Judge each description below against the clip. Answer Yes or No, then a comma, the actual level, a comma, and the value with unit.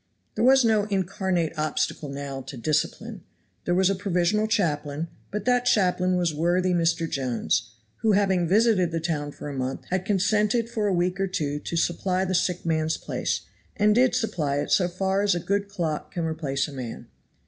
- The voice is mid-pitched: Yes, medium, 180 Hz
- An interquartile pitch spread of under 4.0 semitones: No, average, 4.4 semitones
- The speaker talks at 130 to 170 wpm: No, average, 190 wpm